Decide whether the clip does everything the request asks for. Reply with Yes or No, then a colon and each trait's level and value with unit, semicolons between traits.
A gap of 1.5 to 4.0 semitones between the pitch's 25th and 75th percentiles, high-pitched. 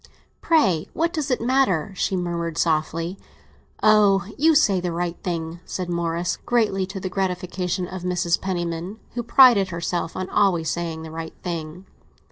No: average, 2.8 semitones; medium, 180 Hz